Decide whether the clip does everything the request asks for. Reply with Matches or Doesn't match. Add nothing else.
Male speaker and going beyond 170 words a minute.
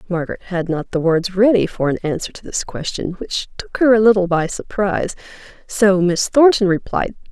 Doesn't match